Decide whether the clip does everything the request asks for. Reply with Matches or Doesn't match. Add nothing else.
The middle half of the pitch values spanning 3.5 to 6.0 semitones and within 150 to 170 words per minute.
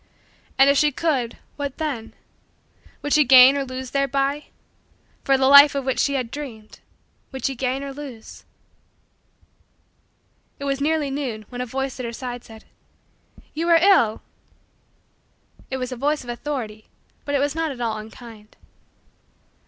Doesn't match